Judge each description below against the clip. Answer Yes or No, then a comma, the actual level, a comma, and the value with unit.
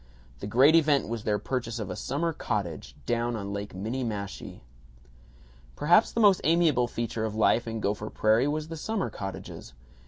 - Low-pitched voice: Yes, low, 115 Hz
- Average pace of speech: Yes, average, 165 wpm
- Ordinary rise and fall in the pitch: No, wide, 6.1 semitones